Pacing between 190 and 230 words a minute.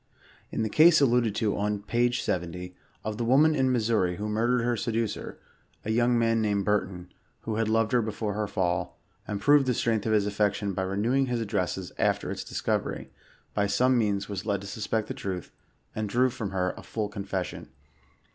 Yes: average, 195 wpm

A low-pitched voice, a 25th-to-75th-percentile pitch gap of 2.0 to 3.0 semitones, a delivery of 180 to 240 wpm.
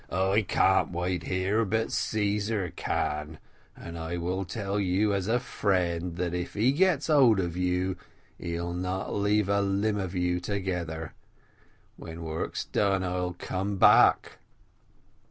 No: very low, 95 Hz; narrow, 2.5 semitones; average, 140 wpm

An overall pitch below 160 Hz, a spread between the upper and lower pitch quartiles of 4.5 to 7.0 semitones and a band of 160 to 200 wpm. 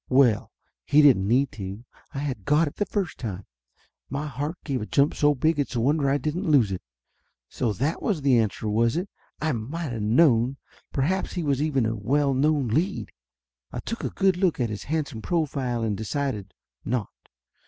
Yes: low, 135 Hz; average, 5.0 semitones; average, 195 wpm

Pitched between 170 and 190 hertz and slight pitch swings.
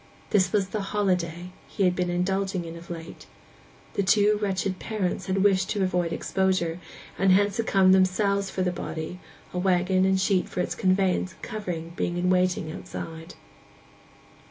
Yes: medium, 185 Hz; narrow, 1.7 semitones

